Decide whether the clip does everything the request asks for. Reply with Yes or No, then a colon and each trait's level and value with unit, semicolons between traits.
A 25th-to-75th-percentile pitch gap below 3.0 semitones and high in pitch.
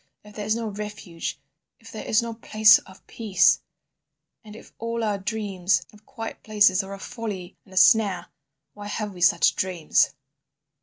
Yes: narrow, 2.6 semitones; high, 210 Hz